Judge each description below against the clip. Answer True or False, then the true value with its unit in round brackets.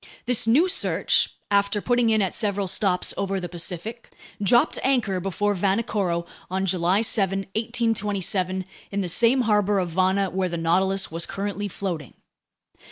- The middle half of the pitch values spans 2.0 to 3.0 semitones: True (2.7 semitones)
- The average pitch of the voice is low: False (195 Hz)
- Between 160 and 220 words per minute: False (150 wpm)